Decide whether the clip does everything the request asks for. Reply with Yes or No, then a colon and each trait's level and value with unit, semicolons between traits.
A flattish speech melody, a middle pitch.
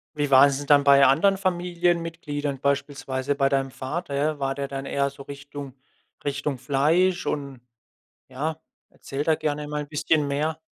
Yes: narrow, 2.1 semitones; medium, 145 Hz